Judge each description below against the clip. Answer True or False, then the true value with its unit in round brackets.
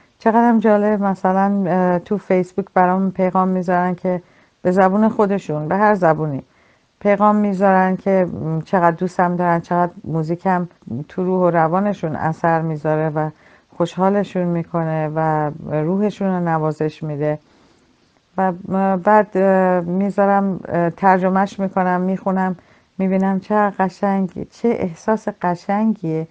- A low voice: False (185 Hz)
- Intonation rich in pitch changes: False (2.6 semitones)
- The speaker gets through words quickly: False (110 wpm)